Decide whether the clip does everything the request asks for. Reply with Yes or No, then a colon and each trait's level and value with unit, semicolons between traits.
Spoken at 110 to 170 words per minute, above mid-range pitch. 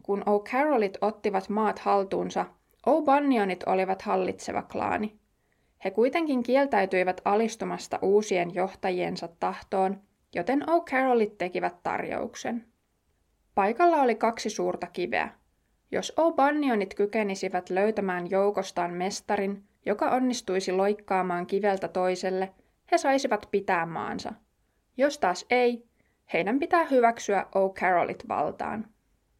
No: average, 100 wpm; high, 205 Hz